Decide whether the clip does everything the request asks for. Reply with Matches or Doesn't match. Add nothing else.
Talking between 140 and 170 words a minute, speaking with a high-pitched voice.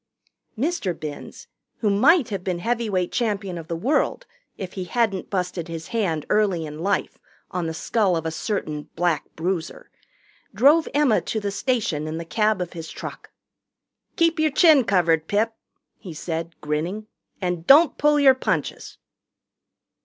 Matches